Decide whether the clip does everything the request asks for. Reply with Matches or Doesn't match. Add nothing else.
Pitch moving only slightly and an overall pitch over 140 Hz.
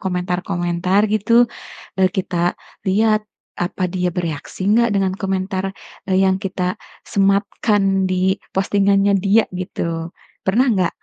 Matches